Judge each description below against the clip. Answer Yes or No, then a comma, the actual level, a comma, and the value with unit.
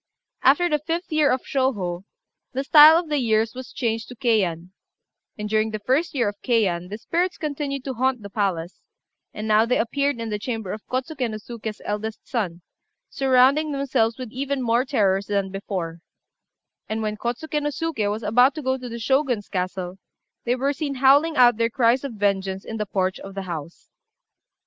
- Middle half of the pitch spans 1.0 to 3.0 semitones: No, average, 4.7 semitones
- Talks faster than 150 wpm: Yes, average, 190 wpm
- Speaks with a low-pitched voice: No, high, 230 Hz